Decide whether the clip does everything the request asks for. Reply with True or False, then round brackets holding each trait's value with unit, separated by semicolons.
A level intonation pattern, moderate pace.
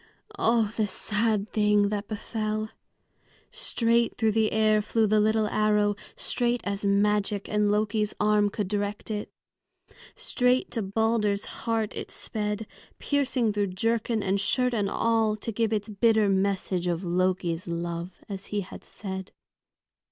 True (1.7 semitones; 145 wpm)